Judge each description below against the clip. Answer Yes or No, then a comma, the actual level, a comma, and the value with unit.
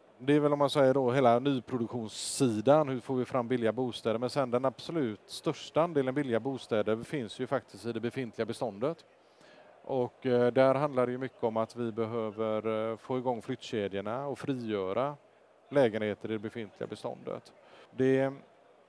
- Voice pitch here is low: Yes, low, 125 Hz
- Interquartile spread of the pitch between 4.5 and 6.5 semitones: No, average, 3.0 semitones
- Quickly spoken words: No, average, 160 wpm